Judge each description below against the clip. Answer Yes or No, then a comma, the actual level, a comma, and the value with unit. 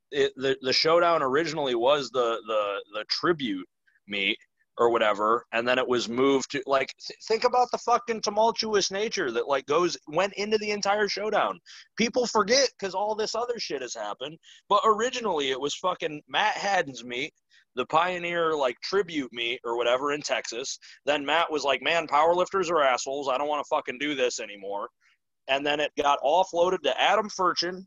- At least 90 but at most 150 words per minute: No, average, 185 wpm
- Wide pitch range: Yes, wide, 7.7 semitones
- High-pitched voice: No, medium, 170 Hz